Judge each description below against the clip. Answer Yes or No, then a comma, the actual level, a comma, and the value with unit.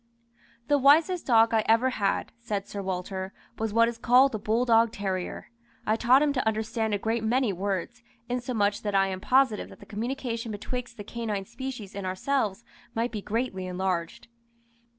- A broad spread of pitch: No, average, 3.5 semitones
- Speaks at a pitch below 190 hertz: No, high, 225 Hz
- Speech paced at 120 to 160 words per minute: No, average, 170 wpm